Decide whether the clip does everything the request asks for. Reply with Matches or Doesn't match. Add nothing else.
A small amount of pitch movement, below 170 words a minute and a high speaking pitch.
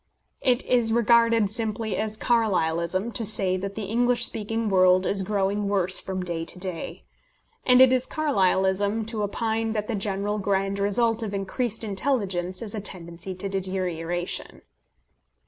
Doesn't match